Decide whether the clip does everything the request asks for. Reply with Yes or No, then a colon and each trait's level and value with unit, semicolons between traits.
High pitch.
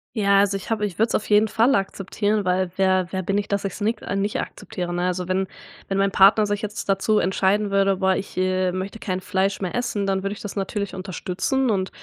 Yes: high, 195 Hz